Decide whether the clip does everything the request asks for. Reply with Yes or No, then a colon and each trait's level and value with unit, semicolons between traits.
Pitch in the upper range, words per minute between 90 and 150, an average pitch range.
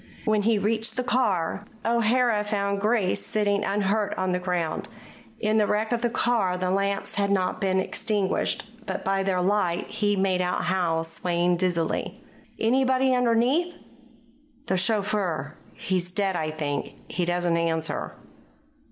Yes: high, 200 Hz; average, 145 wpm; average, 3.3 semitones